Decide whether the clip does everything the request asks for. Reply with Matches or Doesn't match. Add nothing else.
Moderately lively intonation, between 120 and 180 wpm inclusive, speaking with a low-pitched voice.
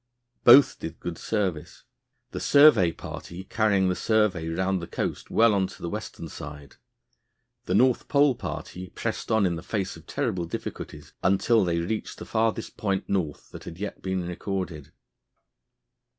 Matches